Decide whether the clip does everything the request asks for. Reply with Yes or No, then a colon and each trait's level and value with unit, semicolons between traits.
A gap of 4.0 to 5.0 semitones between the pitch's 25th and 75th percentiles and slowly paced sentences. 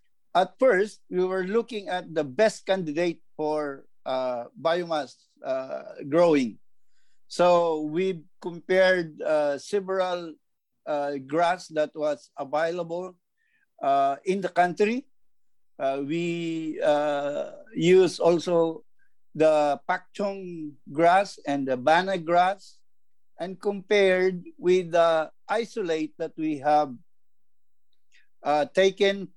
No: average, 3.6 semitones; slow, 100 wpm